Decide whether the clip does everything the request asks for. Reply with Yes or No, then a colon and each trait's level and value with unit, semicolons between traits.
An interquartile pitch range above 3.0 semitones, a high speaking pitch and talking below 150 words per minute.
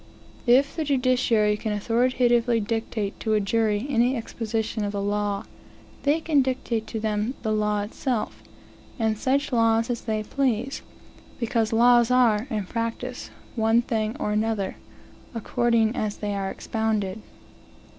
No: narrow, 2.4 semitones; high, 225 Hz; average, 140 wpm